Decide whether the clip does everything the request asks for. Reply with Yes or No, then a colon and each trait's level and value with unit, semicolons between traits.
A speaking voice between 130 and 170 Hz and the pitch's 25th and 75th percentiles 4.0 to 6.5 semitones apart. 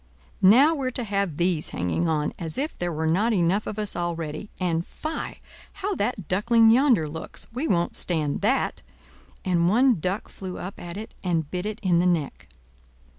No: medium, 185 Hz; average, 4.8 semitones